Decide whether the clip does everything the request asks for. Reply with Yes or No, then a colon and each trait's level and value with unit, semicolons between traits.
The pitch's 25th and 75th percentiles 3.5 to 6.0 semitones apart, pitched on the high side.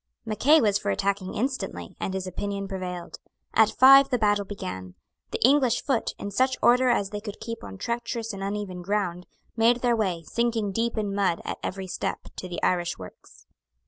Yes: average, 3.9 semitones; high, 205 Hz